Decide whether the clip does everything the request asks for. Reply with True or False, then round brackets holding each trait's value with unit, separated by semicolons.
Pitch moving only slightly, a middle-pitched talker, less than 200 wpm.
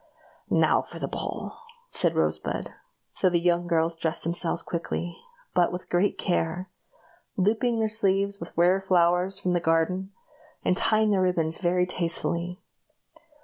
True (2.1 semitones; 180 Hz; 145 wpm)